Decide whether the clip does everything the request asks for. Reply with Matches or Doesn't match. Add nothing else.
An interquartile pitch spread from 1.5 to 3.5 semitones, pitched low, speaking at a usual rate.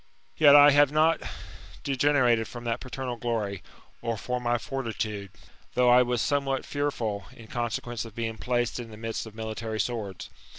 Matches